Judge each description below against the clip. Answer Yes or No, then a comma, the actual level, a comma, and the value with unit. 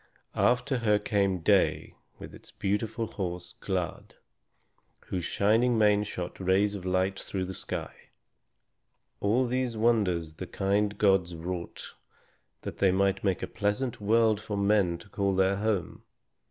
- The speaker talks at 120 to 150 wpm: Yes, average, 140 wpm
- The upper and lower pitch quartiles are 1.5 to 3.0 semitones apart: Yes, narrow, 2.5 semitones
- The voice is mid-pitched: No, low, 100 Hz